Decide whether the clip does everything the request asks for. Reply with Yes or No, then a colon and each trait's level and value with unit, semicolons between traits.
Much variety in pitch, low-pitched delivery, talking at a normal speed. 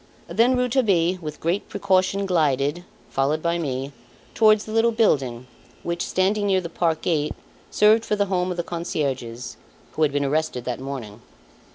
No: wide, 6.0 semitones; medium, 170 Hz; average, 165 wpm